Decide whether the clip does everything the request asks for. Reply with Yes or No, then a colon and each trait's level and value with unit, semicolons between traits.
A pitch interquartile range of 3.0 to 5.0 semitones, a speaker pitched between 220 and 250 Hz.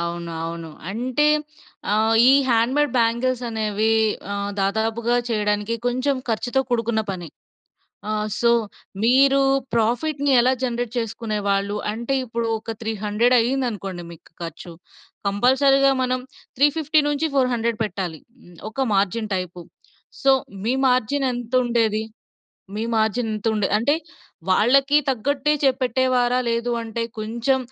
Yes: average, 3.3 semitones; high, 230 Hz